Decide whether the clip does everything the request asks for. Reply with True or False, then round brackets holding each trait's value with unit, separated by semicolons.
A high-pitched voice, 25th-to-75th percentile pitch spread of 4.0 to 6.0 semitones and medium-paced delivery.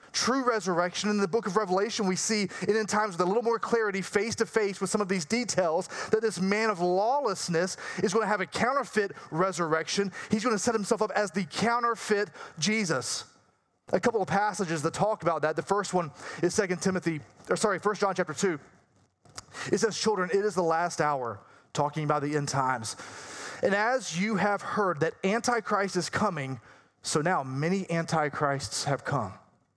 True (195 Hz; 4.3 semitones; 190 wpm)